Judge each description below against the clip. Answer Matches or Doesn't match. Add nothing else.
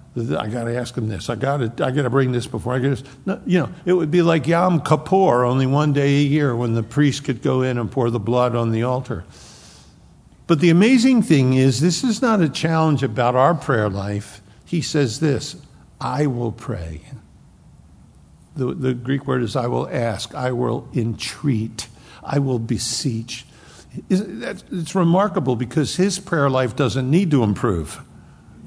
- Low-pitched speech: Matches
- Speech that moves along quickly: Doesn't match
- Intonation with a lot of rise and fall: Doesn't match